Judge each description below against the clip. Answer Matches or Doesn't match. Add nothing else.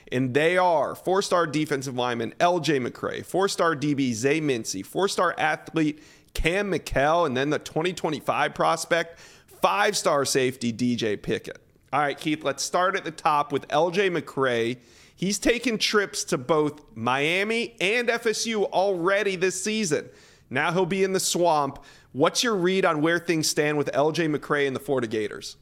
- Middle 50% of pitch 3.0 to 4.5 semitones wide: Doesn't match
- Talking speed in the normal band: Matches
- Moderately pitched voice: Matches